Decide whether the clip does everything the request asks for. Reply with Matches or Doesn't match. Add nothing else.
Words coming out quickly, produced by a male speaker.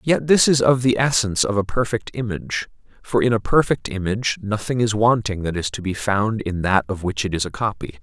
Matches